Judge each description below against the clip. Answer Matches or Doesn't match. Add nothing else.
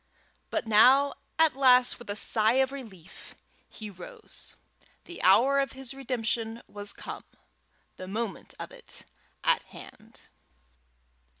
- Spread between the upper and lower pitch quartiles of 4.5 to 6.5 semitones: Doesn't match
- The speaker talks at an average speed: Doesn't match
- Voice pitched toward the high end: Matches